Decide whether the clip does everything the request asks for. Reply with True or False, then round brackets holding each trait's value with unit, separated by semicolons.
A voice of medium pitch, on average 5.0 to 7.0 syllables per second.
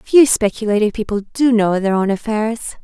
False (220 Hz; 5.1 syllables/s)